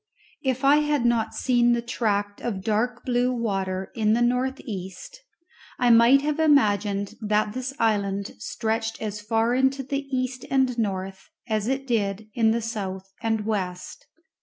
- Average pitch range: Yes, average, 3.7 semitones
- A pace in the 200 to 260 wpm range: No, average, 160 wpm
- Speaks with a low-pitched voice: No, high, 230 Hz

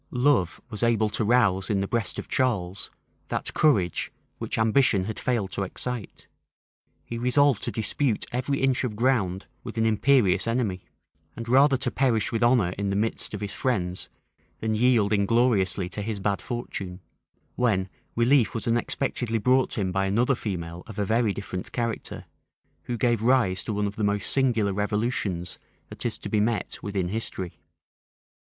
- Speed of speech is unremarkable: Yes, average, 170 wpm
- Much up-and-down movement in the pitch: No, average, 3.8 semitones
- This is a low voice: Yes, low, 110 Hz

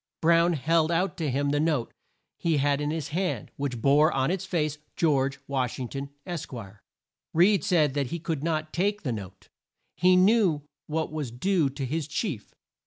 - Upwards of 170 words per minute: Yes, average, 180 wpm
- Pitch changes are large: No, average, 3.5 semitones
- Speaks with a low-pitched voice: No, medium, 155 Hz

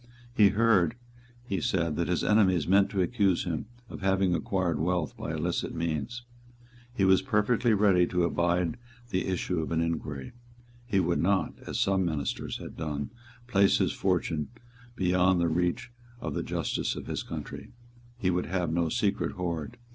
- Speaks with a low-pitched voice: Yes, very low, 90 Hz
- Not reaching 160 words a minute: No, average, 165 wpm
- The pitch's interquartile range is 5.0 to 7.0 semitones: No, average, 2.8 semitones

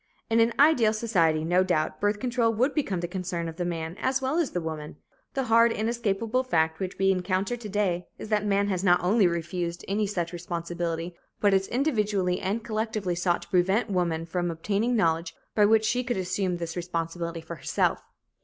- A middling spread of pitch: Yes, average, 4.2 semitones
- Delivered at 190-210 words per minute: Yes, average, 195 wpm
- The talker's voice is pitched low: No, high, 190 Hz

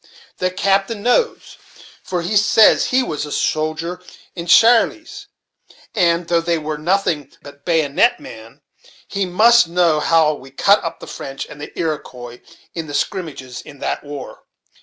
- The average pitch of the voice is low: No, medium, 170 Hz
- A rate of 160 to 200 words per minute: No, average, 150 wpm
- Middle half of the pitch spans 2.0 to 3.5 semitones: No, average, 4.9 semitones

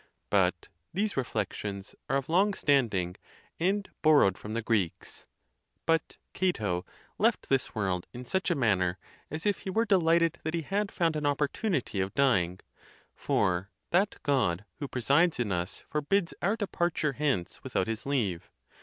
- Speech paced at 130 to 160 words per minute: Yes, average, 155 wpm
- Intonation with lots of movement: Yes, wide, 8.9 semitones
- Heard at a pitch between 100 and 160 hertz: Yes, medium, 140 Hz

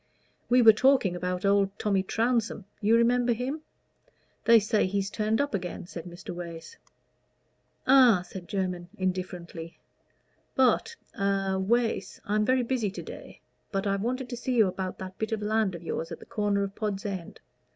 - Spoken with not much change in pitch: No, average, 3.7 semitones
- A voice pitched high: Yes, high, 205 Hz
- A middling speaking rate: Yes, average, 170 wpm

